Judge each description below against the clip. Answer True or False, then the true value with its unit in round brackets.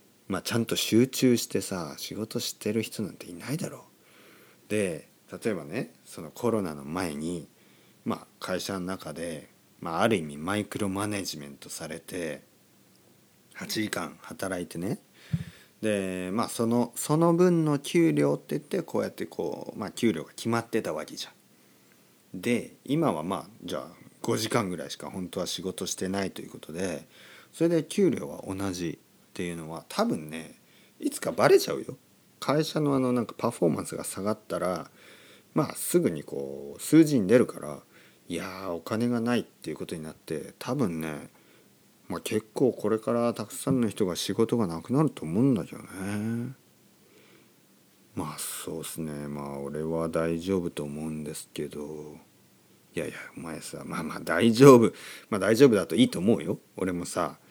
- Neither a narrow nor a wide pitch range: False (6.6 semitones)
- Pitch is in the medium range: False (105 Hz)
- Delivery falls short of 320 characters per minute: True (300 characters per minute)